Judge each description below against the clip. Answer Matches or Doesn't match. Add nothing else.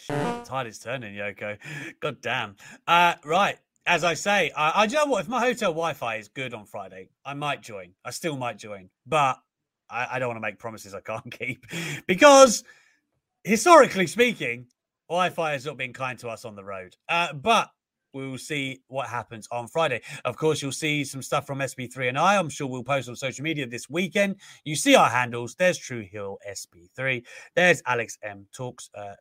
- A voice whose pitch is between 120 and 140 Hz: Matches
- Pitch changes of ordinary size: Doesn't match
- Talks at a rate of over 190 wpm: Matches